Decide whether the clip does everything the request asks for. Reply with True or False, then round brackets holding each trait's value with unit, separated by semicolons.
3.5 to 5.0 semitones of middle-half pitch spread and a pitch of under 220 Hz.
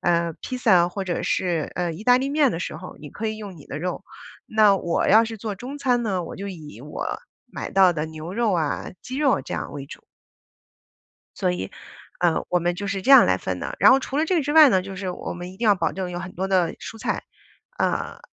True (4.7 semitones; 190 Hz)